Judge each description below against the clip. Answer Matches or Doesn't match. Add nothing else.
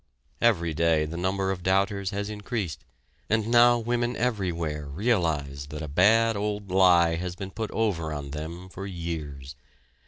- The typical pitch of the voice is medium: Doesn't match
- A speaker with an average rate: Matches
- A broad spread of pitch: Doesn't match